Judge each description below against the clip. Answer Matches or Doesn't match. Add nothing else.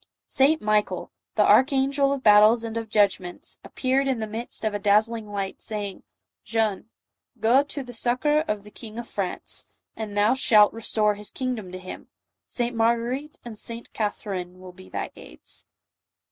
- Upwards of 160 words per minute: Matches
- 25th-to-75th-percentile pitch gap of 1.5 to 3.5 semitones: Matches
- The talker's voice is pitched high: Matches